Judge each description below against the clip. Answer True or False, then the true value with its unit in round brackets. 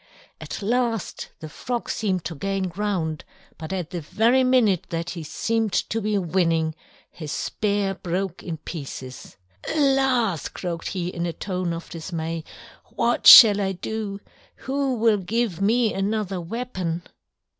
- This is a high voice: True (195 Hz)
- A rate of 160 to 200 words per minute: False (145 wpm)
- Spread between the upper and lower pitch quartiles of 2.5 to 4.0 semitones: False (4.8 semitones)